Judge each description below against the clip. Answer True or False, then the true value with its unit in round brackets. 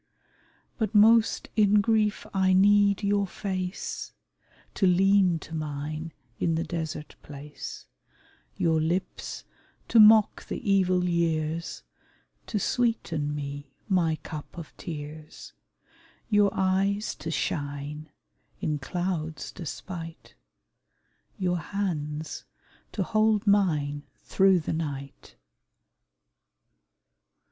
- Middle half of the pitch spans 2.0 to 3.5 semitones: False (4.5 semitones)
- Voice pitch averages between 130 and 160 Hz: False (175 Hz)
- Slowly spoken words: True (100 wpm)